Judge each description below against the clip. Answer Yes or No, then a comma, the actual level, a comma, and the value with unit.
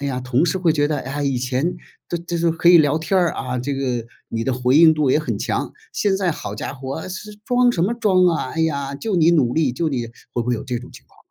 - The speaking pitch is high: No, medium, 150 Hz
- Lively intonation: No, average, 5.0 semitones